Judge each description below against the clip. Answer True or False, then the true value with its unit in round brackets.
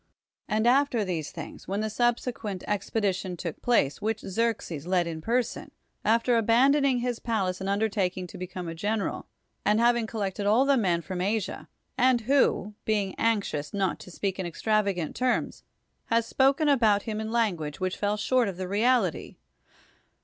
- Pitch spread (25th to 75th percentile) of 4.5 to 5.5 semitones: False (3.9 semitones)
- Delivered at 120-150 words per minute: False (170 wpm)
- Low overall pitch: False (210 Hz)